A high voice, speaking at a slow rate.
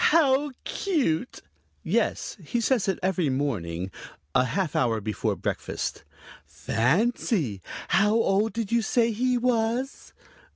Yes: high, 210 Hz; slow, 120 wpm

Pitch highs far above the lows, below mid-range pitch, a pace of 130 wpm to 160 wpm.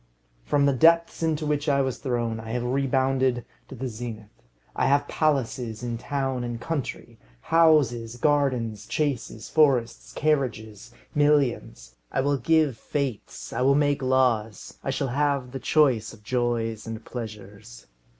No: average, 3.8 semitones; low, 130 Hz; average, 145 wpm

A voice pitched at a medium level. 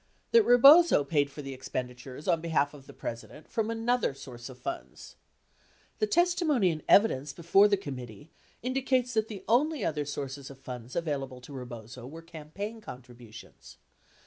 Yes: medium, 150 Hz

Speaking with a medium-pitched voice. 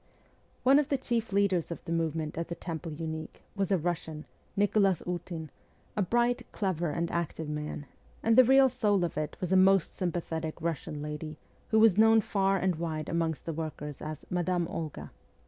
Yes: medium, 170 Hz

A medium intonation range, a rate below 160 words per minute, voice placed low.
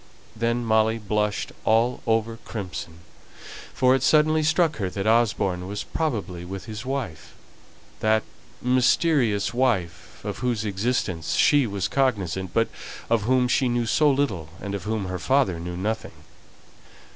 Yes: average, 4.5 semitones; average, 145 wpm; low, 110 Hz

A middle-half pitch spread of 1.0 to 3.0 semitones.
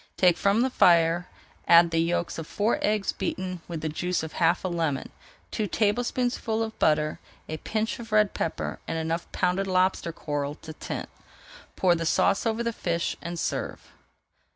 No: average, 4.4 semitones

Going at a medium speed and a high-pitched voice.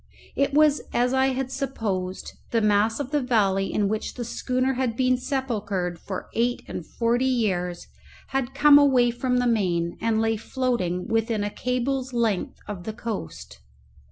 Yes: average, 165 wpm; high, 235 Hz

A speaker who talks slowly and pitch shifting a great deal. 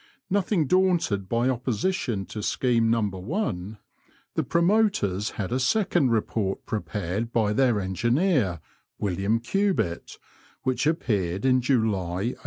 Yes: slow, 120 wpm; wide, 6.1 semitones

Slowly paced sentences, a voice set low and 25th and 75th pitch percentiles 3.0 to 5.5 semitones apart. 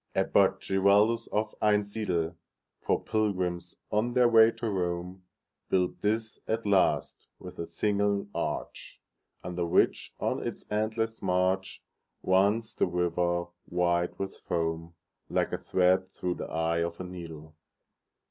Yes: slow, 115 wpm; very low, 95 Hz; average, 3.3 semitones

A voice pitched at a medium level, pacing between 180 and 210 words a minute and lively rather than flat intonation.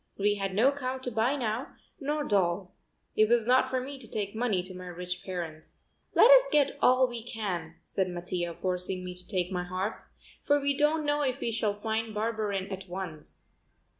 No: high, 210 Hz; average, 195 wpm; wide, 5.7 semitones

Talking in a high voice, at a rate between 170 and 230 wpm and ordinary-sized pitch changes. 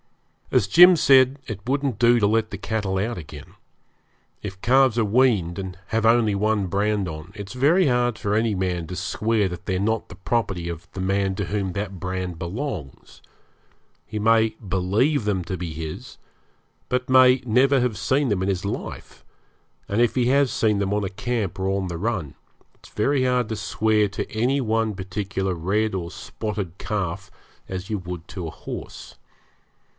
No: low, 105 Hz; average, 185 wpm; average, 3.9 semitones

